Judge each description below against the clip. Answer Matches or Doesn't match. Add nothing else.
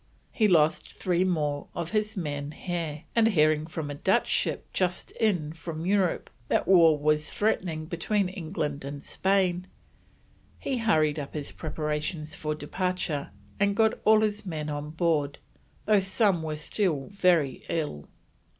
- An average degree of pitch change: Matches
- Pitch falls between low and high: Matches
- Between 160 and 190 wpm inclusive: Doesn't match